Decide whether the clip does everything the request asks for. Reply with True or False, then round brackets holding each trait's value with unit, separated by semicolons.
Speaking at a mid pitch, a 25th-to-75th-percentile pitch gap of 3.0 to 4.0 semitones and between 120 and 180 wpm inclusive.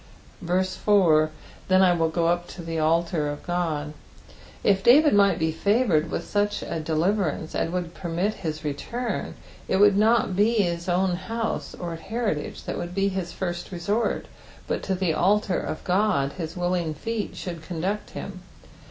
True (180 Hz; 3.6 semitones; 160 wpm)